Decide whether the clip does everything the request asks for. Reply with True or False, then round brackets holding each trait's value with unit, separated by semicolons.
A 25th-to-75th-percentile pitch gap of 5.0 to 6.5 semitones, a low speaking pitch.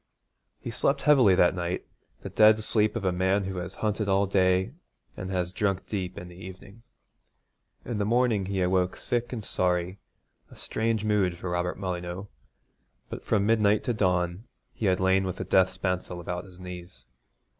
False (2.6 semitones; 95 Hz)